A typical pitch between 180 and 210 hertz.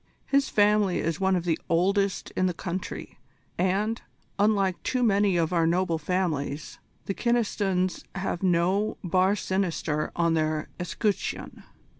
Yes: medium, 185 Hz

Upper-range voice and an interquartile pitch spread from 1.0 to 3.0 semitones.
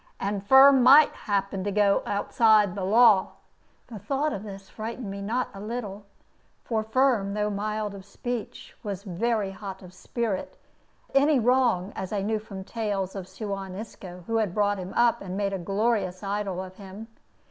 Yes: high, 205 Hz; average, 2.7 semitones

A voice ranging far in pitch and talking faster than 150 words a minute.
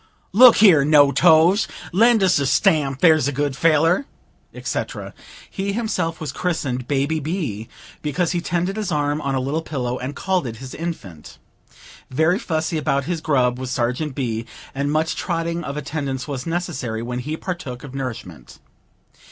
No: average, 4.4 semitones; average, 165 wpm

